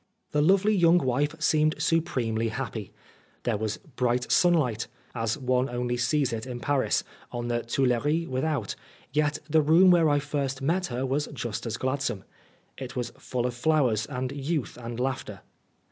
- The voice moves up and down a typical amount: Yes, average, 4.0 semitones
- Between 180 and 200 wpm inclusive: No, average, 165 wpm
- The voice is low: Yes, low, 130 Hz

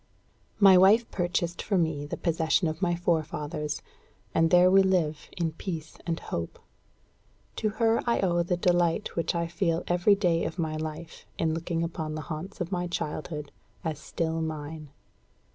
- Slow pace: No, average, 165 wpm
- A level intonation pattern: Yes, narrow, 2.2 semitones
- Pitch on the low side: No, medium, 170 Hz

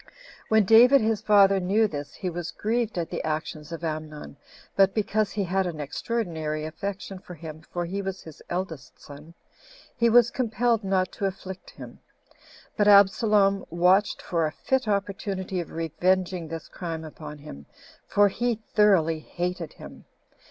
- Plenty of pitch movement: No, average, 4.2 semitones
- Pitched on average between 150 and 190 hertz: Yes, medium, 185 Hz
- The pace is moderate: Yes, average, 160 wpm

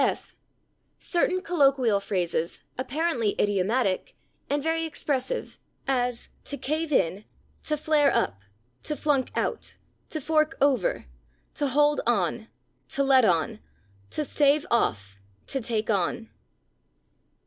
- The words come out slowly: Yes, slow, 115 wpm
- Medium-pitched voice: No, very high, 265 Hz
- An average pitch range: No, wide, 6.0 semitones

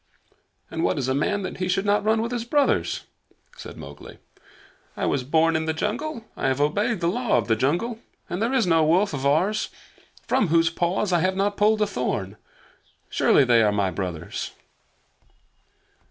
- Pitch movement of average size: No, wide, 6.9 semitones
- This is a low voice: No, medium, 175 Hz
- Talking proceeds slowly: No, average, 185 wpm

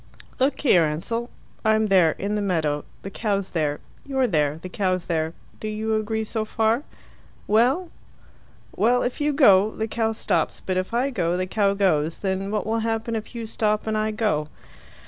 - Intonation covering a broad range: No, average, 3.5 semitones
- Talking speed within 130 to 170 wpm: No, average, 185 wpm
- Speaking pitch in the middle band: No, high, 215 Hz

